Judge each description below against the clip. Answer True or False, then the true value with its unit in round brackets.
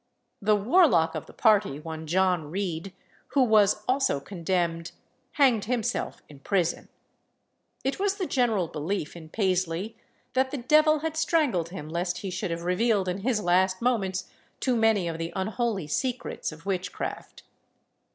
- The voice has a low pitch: False (195 Hz)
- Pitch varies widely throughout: True (6.0 semitones)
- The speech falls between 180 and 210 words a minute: False (150 wpm)